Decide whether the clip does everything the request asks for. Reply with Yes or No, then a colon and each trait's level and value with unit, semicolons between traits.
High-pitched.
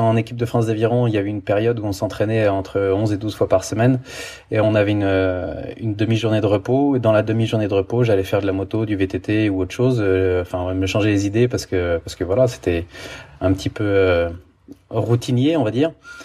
No: low, 105 Hz